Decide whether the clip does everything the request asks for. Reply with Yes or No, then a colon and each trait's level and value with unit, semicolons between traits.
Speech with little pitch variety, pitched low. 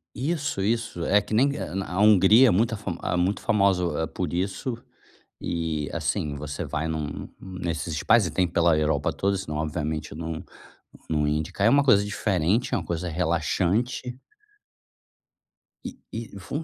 No: average, 5.1 semitones; very low, 90 Hz